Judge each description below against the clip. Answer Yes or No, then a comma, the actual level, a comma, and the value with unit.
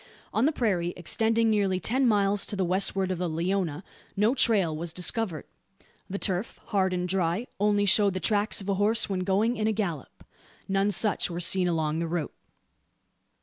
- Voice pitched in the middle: No, high, 195 Hz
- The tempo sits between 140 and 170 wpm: No, average, 185 wpm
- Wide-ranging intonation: No, average, 3.0 semitones